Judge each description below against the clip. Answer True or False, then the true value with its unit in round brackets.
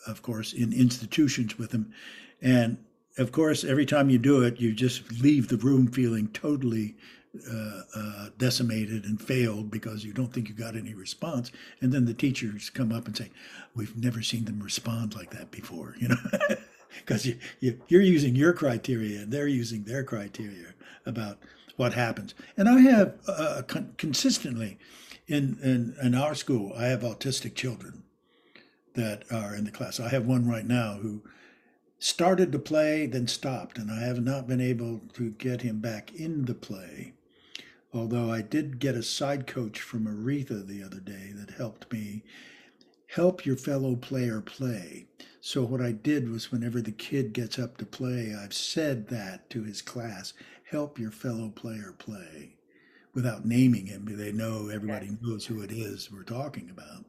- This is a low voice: True (120 Hz)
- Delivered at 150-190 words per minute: True (175 wpm)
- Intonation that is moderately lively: True (3.0 semitones)